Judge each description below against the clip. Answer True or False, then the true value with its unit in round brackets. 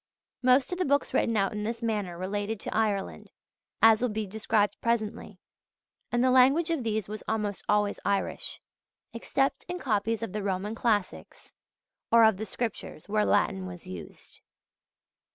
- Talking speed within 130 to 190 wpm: True (160 wpm)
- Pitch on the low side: False (215 Hz)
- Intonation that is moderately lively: False (2.3 semitones)